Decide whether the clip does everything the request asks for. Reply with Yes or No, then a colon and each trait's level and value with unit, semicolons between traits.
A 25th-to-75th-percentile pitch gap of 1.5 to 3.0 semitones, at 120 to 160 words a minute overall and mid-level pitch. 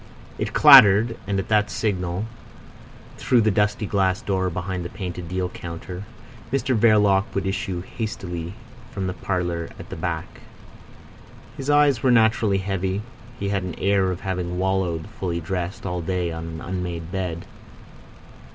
No: narrow, 2.6 semitones; average, 150 wpm; very low, 95 Hz